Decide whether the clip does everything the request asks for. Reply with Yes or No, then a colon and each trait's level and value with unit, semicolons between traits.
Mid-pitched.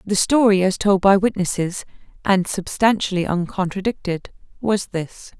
No: high, 195 Hz